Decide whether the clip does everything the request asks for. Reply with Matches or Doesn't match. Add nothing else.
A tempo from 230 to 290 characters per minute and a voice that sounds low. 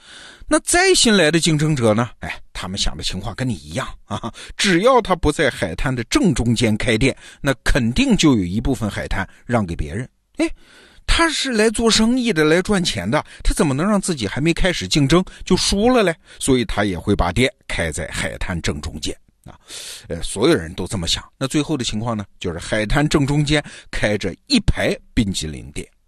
Matches